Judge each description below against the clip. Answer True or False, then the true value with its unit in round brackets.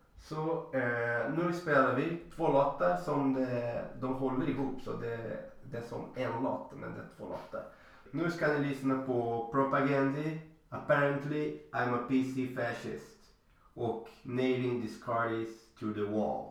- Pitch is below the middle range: True (130 Hz)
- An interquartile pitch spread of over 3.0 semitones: True (3.5 semitones)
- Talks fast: False (155 wpm)